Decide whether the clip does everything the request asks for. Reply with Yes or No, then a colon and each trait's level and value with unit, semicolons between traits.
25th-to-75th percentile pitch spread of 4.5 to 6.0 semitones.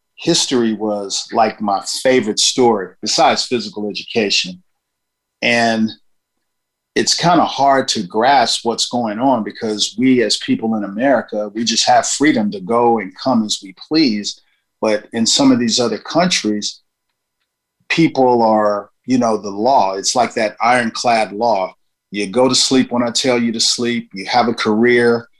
No: average, 3.5 semitones